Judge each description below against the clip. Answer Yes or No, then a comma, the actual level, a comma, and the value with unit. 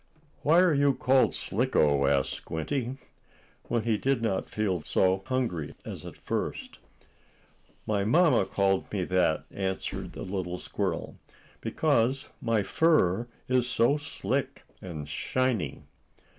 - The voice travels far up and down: Yes, wide, 5.8 semitones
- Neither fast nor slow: No, slow, 130 wpm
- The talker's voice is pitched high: No, low, 110 Hz